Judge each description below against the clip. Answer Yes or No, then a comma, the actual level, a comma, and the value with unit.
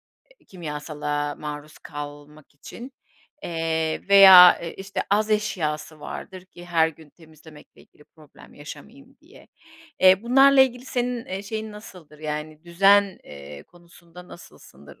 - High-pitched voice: No, medium, 170 Hz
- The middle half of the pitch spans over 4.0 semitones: Yes, average, 5.1 semitones